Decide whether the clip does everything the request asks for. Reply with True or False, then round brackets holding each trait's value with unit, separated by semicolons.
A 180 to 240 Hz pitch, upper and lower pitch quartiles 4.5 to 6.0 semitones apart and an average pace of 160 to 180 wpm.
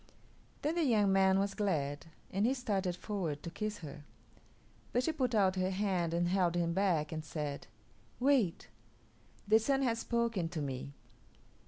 True (190 Hz; 5.2 semitones; 165 wpm)